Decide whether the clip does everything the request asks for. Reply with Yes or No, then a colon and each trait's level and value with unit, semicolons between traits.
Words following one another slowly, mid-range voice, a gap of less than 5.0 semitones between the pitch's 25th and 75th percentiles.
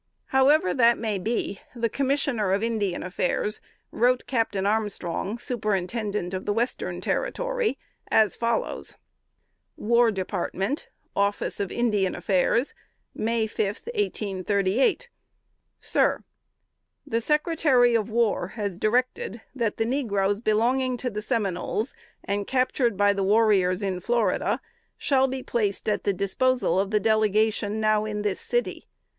No: slow, 125 wpm; high, 220 Hz; average, 3.3 semitones